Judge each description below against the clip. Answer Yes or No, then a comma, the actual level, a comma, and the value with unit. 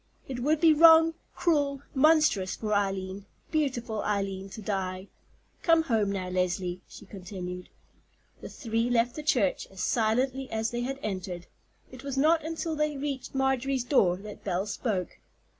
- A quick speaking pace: No, average, 155 wpm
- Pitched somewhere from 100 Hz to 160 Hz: No, high, 230 Hz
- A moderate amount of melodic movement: No, wide, 6.3 semitones